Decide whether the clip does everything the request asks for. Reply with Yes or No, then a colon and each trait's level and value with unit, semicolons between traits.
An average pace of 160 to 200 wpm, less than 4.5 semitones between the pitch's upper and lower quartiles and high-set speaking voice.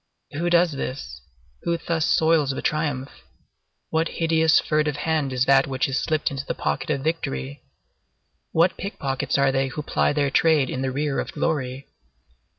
No: average, 165 wpm; average, 3.1 semitones; medium, 145 Hz